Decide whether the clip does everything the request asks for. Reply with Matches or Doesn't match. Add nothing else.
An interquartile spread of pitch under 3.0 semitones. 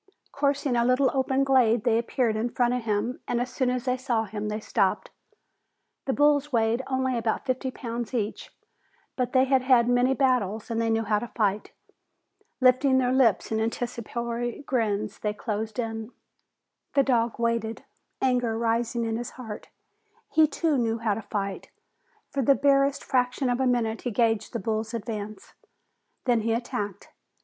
Matches